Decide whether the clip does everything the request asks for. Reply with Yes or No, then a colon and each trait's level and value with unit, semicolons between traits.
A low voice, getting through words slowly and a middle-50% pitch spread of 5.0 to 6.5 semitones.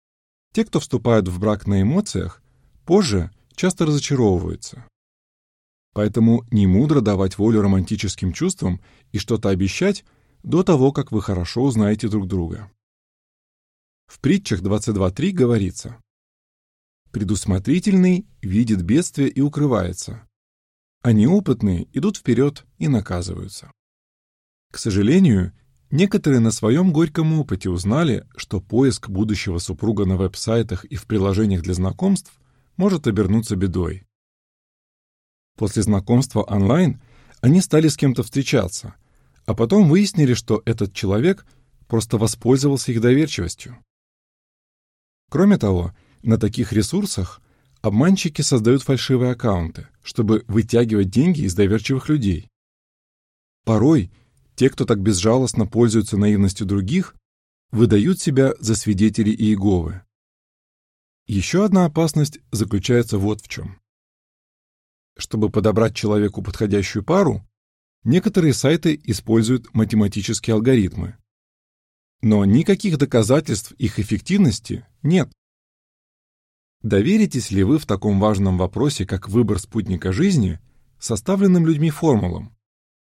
Yes: low, 110 Hz; slow, 105 wpm; wide, 5.4 semitones